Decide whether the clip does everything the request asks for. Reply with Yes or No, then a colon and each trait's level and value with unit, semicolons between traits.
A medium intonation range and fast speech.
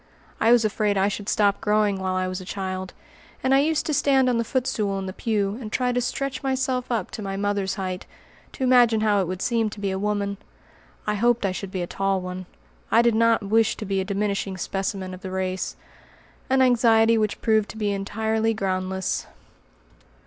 Yes: average, 3.1 semitones; fast, 210 wpm